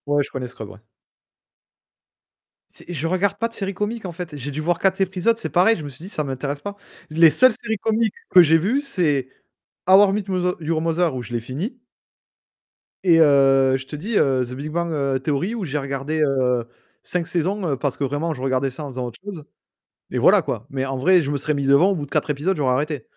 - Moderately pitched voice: Yes, medium, 155 Hz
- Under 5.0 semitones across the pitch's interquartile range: No, wide, 5.4 semitones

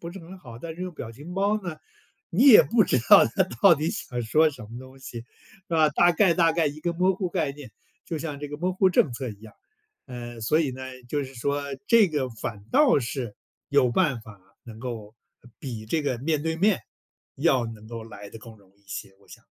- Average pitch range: No, wide, 6.4 semitones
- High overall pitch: No, medium, 145 Hz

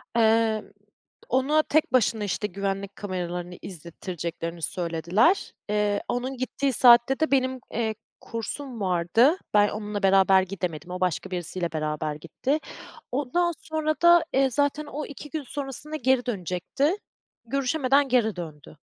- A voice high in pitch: Yes, high, 220 Hz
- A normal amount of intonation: No, wide, 6.9 semitones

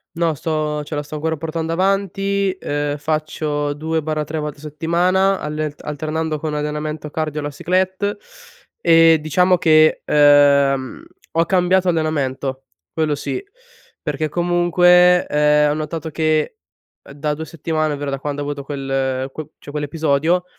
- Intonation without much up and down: Yes, narrow, 2.1 semitones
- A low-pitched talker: No, medium, 155 Hz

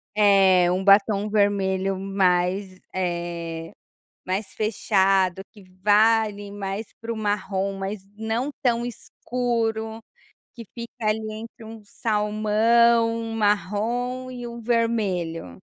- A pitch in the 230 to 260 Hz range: No, high, 210 Hz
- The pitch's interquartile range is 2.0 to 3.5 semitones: Yes, average, 2.9 semitones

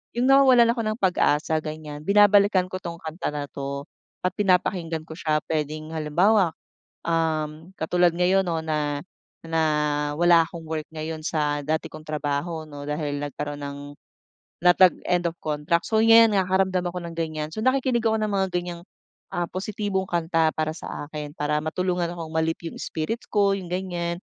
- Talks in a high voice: No, medium, 165 Hz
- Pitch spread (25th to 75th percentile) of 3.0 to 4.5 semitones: Yes, average, 3.3 semitones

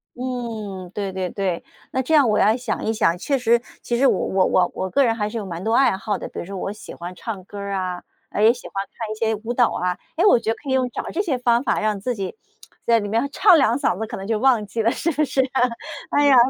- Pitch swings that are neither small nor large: Yes, average, 4.2 semitones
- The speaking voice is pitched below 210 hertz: No, high, 225 Hz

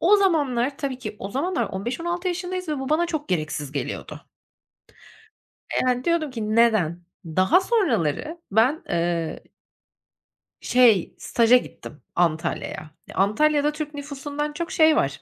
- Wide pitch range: Yes, wide, 8.4 semitones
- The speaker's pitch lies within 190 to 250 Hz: No, very high, 260 Hz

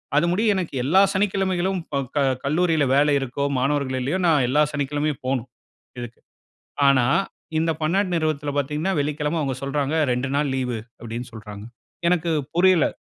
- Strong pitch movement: No, average, 4.2 semitones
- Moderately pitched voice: Yes, medium, 150 Hz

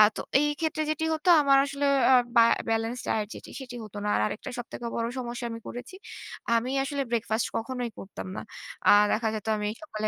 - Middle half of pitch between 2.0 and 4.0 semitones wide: Yes, average, 3.6 semitones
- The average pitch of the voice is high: Yes, high, 240 Hz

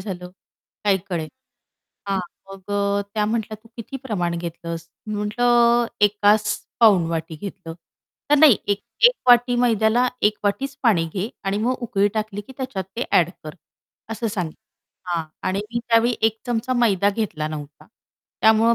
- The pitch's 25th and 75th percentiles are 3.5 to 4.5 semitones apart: Yes, average, 3.9 semitones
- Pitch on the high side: Yes, high, 210 Hz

